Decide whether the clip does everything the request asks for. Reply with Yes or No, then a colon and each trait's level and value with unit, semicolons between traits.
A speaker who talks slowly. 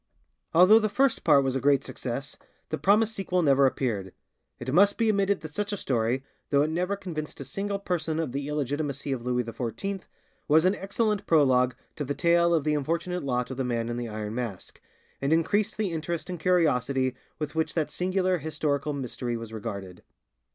No: average, 195 wpm